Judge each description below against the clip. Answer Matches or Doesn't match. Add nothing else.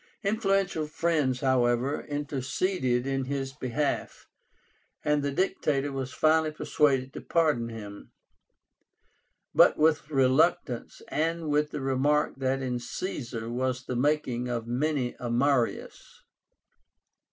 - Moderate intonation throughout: Matches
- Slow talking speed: Matches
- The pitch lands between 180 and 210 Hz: Doesn't match